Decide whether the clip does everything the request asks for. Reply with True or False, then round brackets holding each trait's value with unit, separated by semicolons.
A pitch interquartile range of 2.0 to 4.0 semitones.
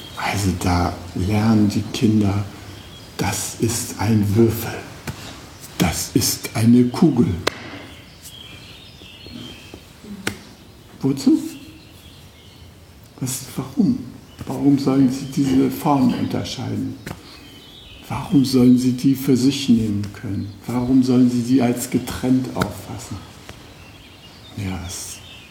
False (4.7 semitones)